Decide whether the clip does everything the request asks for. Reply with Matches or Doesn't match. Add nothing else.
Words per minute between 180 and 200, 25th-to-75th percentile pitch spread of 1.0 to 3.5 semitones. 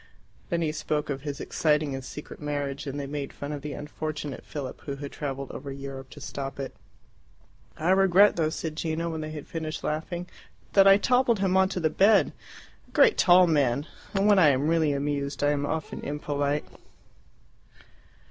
Matches